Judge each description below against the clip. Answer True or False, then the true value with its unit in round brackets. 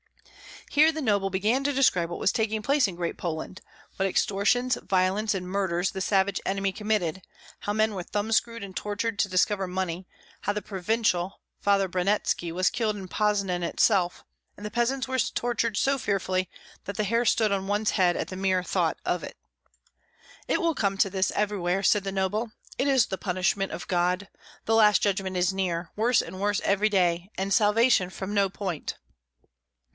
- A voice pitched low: False (200 Hz)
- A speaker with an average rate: True (180 wpm)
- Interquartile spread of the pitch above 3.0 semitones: False (2.6 semitones)